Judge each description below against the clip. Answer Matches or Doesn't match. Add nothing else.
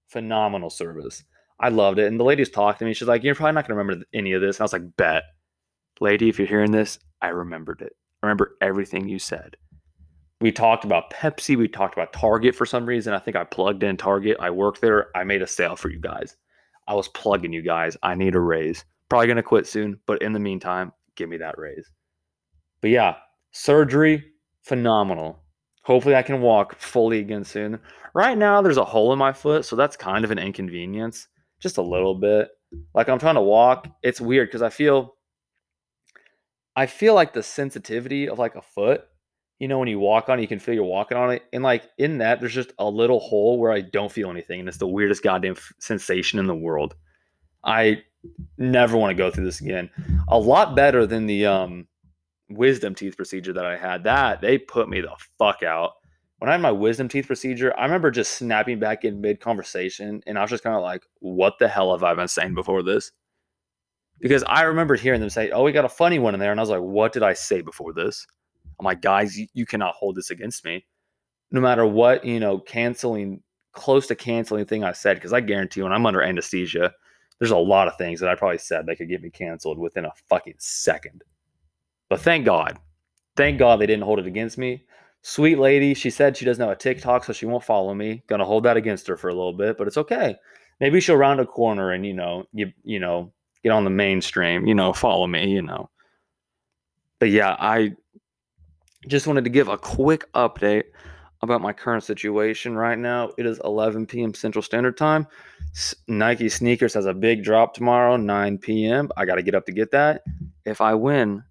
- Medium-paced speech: Doesn't match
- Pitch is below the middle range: Matches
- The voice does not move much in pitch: Doesn't match